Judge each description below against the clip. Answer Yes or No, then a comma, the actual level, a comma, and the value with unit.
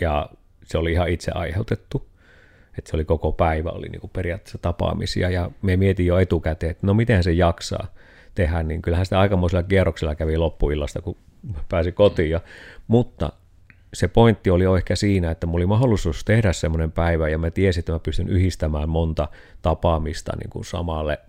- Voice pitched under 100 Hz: Yes, very low, 85 Hz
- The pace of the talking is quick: Yes, fast, 175 wpm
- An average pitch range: Yes, average, 3.0 semitones